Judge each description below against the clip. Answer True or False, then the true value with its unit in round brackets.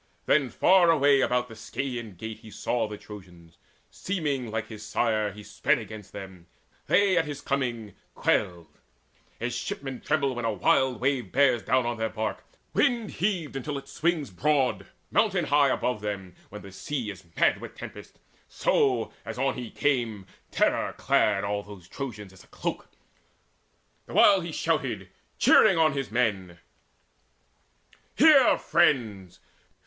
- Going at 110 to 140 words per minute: False (155 wpm)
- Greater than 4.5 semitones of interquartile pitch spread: True (5.3 semitones)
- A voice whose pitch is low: True (120 Hz)